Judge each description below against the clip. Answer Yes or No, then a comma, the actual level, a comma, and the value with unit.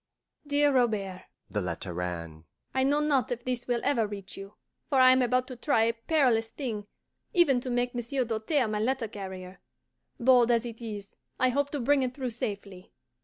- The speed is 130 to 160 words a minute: No, average, 190 wpm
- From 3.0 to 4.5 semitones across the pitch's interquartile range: Yes, average, 4.0 semitones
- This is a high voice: Yes, high, 240 Hz